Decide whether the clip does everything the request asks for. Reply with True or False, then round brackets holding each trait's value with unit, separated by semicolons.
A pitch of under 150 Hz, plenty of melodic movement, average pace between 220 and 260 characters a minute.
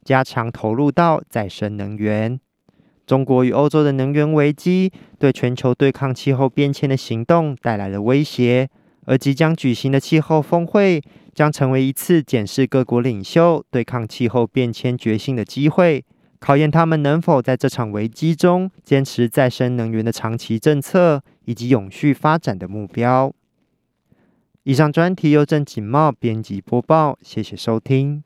False (135 Hz; 4.1 semitones; 245 characters per minute)